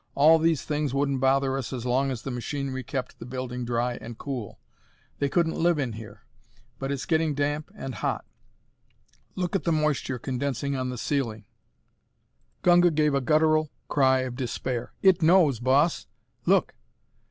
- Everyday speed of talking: Yes, average, 165 wpm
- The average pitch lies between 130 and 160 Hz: Yes, low, 135 Hz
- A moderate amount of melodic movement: Yes, average, 3.3 semitones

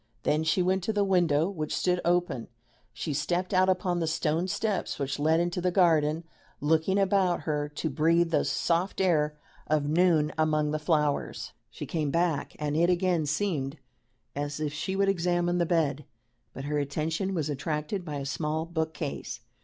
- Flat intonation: No, average, 3.0 semitones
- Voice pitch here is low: No, medium, 160 Hz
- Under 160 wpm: No, average, 175 wpm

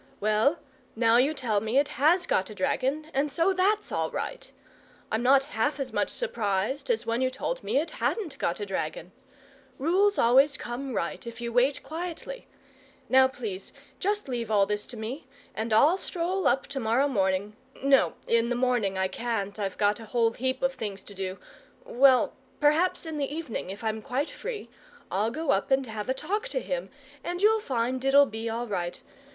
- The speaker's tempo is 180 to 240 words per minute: Yes, average, 190 wpm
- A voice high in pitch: Yes, very high, 255 Hz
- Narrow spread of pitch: No, average, 5.3 semitones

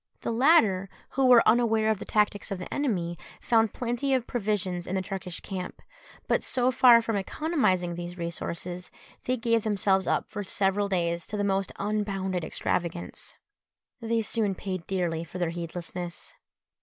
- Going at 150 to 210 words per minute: Yes, average, 160 wpm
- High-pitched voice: Yes, high, 195 Hz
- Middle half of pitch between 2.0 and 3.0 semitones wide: No, average, 4.1 semitones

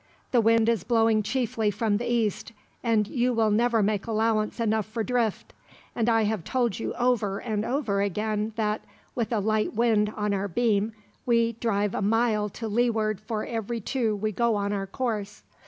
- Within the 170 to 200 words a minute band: Yes, average, 185 wpm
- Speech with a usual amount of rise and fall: No, narrow, 1.8 semitones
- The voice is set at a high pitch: Yes, high, 220 Hz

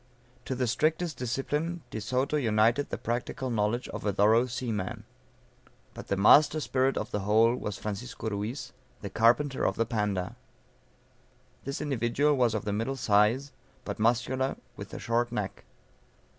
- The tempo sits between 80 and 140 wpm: No, average, 155 wpm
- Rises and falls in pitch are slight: No, average, 3.8 semitones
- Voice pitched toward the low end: Yes, low, 120 Hz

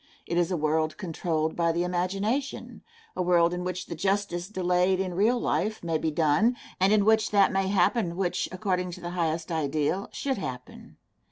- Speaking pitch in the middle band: Yes, medium, 180 Hz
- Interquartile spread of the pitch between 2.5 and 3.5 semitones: Yes, average, 2.8 semitones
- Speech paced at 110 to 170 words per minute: No, average, 185 wpm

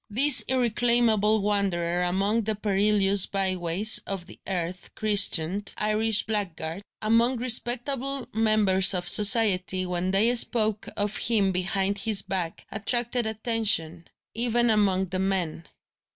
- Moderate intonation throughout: Yes, average, 3.1 semitones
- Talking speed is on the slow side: Yes, slow, 125 wpm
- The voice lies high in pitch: Yes, high, 205 Hz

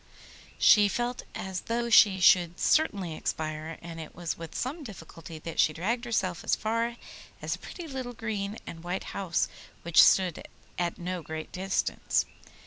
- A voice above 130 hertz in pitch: Yes, medium, 185 Hz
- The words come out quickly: No, average, 160 wpm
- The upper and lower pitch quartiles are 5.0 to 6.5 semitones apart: Yes, wide, 5.5 semitones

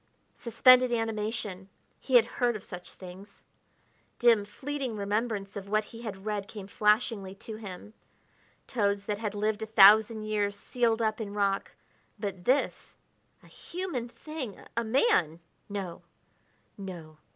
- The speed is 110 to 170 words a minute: Yes, average, 140 wpm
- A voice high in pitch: Yes, high, 215 Hz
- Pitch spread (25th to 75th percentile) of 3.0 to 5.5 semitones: No, narrow, 2.6 semitones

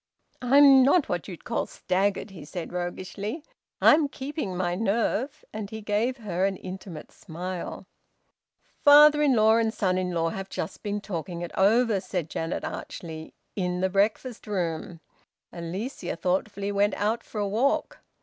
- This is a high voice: Yes, high, 200 Hz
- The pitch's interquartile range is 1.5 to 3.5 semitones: No, average, 4.2 semitones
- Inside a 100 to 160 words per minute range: Yes, average, 155 wpm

